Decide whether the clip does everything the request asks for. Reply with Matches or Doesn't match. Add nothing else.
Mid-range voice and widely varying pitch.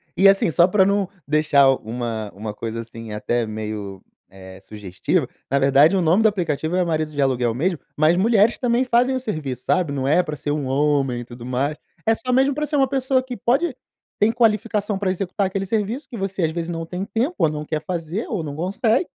Matches